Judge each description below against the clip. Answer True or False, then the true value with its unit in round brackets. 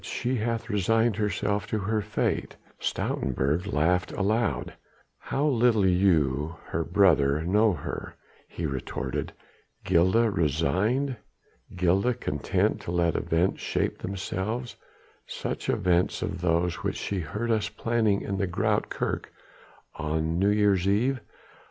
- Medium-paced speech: False (125 wpm)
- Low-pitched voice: True (95 Hz)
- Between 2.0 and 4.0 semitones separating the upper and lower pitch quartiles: False (4.6 semitones)